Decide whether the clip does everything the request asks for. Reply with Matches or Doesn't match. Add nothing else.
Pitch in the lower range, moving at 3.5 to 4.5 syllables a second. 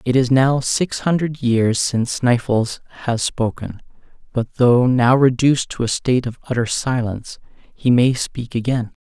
Matches